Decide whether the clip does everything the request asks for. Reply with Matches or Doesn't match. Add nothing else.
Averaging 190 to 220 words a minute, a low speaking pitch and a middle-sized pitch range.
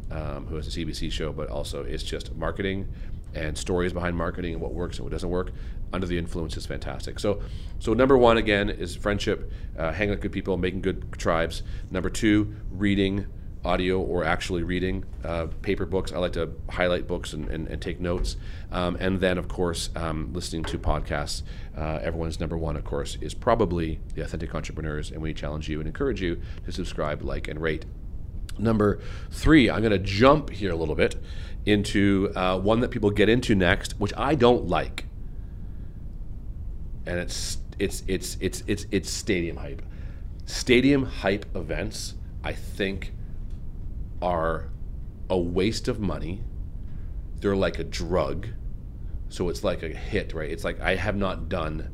Doesn't match